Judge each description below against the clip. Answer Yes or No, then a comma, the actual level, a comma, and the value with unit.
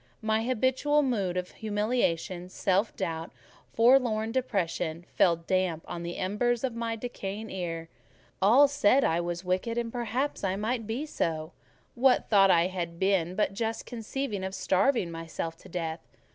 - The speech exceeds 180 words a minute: No, average, 155 wpm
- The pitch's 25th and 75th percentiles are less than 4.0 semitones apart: No, average, 5.2 semitones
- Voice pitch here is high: Yes, high, 200 Hz